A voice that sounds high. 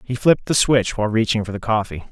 No: low, 115 Hz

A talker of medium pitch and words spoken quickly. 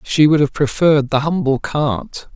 No: medium, 145 Hz; average, 180 wpm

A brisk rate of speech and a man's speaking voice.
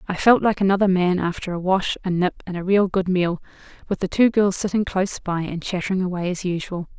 No: fast, 230 wpm; female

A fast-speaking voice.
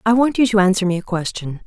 Yes: fast, 290 wpm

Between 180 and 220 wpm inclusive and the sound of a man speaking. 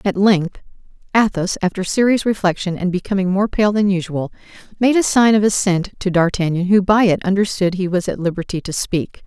No: average, 190 wpm; female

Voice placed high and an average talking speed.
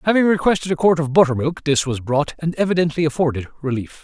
No: medium, 155 Hz; average, 195 wpm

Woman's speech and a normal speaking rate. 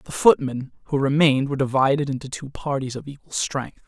No: male; average, 185 wpm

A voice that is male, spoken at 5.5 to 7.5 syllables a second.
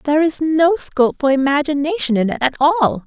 No: female; 5.7 syllables/s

